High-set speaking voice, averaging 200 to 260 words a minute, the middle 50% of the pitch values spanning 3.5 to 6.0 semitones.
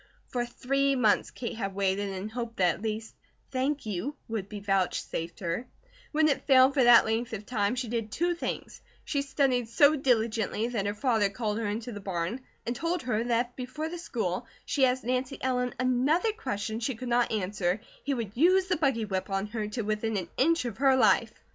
Yes: high, 235 Hz; fast, 205 wpm; average, 4.1 semitones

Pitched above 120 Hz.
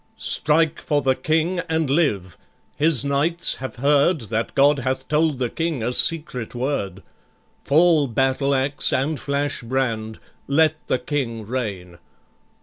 Yes: medium, 140 Hz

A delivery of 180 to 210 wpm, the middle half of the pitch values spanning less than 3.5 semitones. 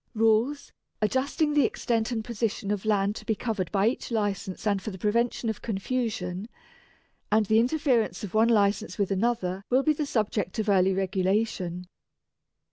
No: average, 165 wpm; average, 3.1 semitones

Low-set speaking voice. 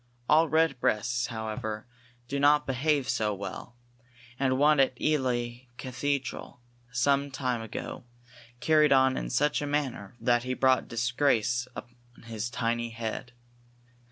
Yes: low, 125 Hz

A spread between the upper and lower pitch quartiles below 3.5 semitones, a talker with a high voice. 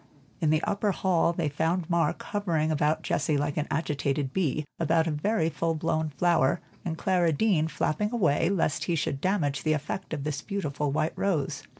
No: average, 3.0 semitones; medium, 160 Hz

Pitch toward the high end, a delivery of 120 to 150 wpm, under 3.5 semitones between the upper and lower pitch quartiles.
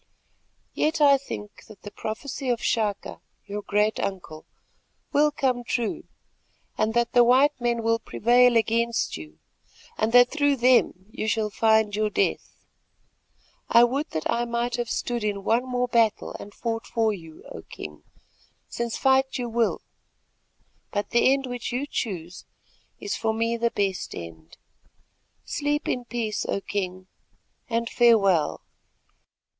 Yes: high, 230 Hz; average, 145 wpm; average, 2.9 semitones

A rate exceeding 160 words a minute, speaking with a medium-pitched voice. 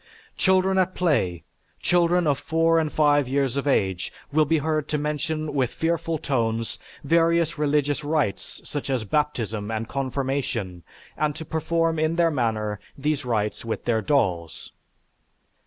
No: average, 145 wpm; medium, 145 Hz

